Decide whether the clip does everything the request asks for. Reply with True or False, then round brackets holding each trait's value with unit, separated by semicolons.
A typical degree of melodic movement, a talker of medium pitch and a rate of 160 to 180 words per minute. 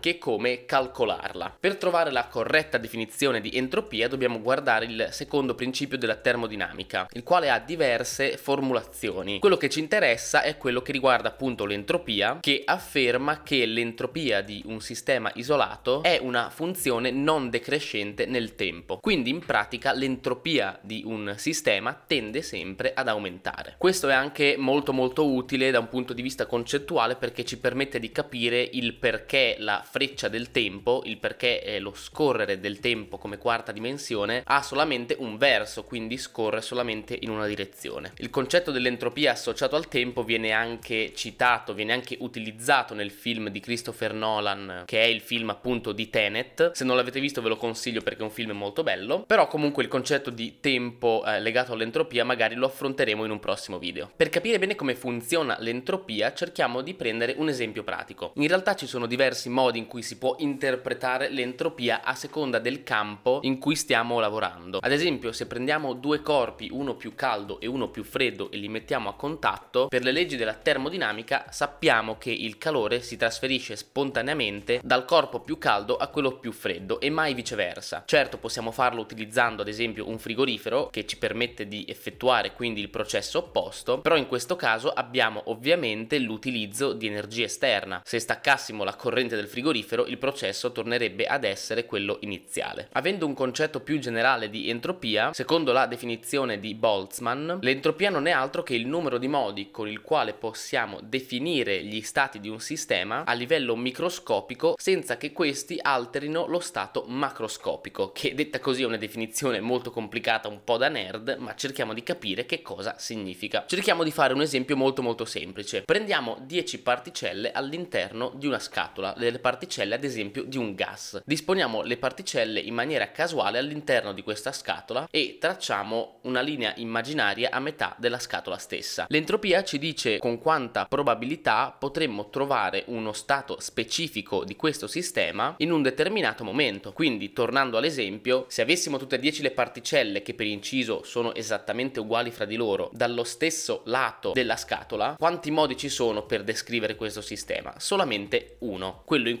False (4.1 semitones; 125 Hz; 170 wpm)